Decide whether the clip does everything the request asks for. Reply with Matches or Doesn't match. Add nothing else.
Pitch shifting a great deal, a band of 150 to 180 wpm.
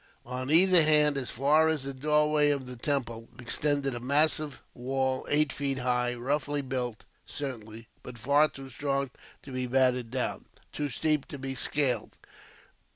Doesn't match